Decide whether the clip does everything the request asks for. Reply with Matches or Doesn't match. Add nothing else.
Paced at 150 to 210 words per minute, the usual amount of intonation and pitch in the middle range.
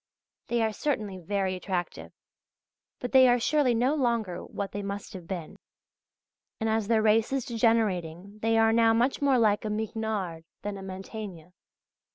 Doesn't match